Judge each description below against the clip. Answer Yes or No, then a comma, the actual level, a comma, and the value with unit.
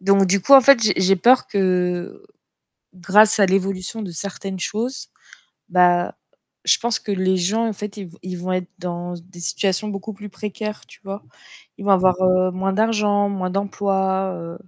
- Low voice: No, high, 195 Hz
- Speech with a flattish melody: Yes, narrow, 2.2 semitones